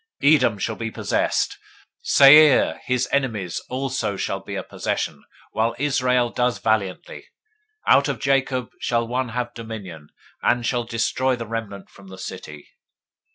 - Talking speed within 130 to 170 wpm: Yes, average, 155 wpm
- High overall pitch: No, low, 120 Hz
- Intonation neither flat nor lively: Yes, average, 3.0 semitones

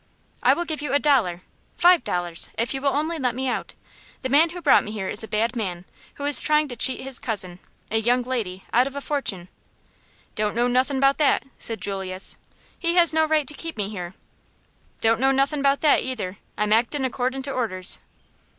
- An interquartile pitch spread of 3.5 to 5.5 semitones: Yes, average, 5.2 semitones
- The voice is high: Yes, very high, 255 Hz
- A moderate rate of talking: No, fast, 210 wpm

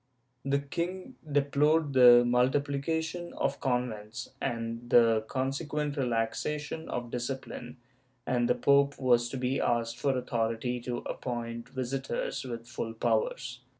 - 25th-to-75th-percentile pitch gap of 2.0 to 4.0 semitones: Yes, average, 2.8 semitones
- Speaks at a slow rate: Yes, slow, 120 wpm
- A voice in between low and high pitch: No, low, 125 Hz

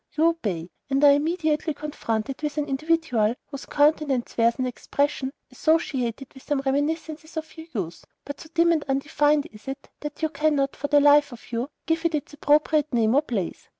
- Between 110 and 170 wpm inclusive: No, average, 185 wpm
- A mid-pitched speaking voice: No, very high, 290 Hz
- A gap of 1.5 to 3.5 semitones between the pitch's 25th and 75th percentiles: Yes, average, 2.8 semitones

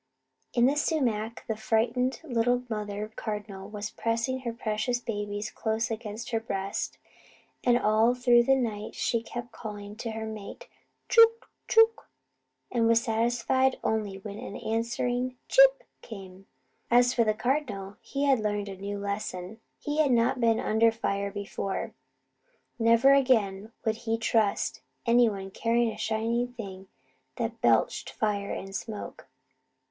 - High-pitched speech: Yes, high, 225 Hz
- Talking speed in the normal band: Yes, average, 145 wpm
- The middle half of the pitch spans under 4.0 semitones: Yes, average, 2.7 semitones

